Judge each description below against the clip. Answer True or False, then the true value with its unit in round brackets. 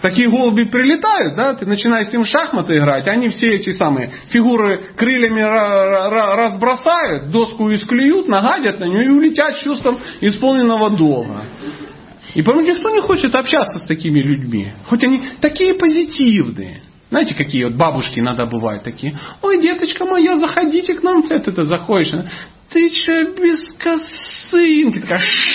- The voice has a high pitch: True (235 Hz)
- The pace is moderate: True (150 wpm)